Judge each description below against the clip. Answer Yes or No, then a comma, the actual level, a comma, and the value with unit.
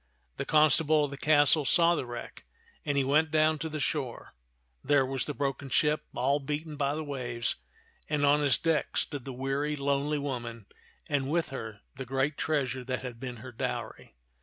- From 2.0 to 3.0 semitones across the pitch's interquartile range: Yes, narrow, 2.4 semitones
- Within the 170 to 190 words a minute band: Yes, average, 185 wpm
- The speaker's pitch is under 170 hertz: Yes, medium, 140 Hz